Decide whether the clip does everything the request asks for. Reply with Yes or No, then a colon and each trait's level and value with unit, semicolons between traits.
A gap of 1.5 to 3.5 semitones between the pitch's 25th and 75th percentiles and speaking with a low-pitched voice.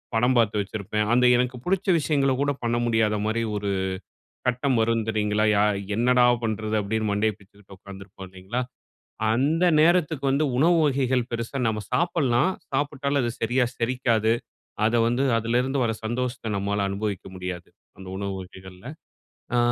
No: average, 4.2 semitones; low, 115 Hz